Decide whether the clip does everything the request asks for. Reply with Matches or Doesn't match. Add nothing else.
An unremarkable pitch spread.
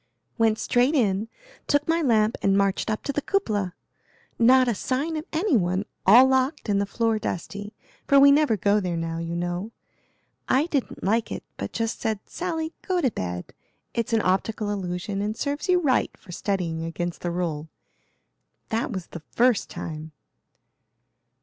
Doesn't match